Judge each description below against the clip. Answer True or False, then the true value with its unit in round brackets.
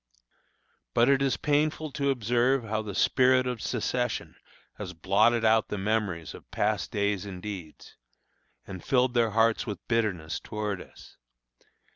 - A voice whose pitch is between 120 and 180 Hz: False (110 Hz)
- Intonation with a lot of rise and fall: False (3.6 semitones)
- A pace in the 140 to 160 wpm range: True (145 wpm)